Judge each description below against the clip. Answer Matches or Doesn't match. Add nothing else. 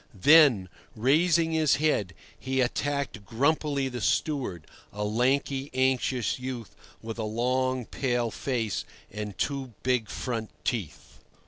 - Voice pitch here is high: Doesn't match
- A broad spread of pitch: Doesn't match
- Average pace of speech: Doesn't match